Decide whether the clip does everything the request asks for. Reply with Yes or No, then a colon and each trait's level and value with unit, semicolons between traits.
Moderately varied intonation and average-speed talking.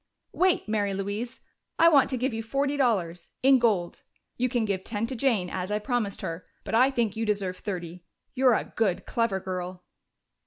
Yes: average, 4.7 semitones; average, 190 wpm